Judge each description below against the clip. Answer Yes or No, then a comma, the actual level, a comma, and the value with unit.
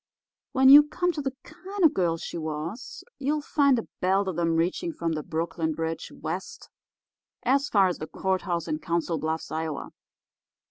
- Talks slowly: No, average, 180 wpm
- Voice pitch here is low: No, medium, 185 Hz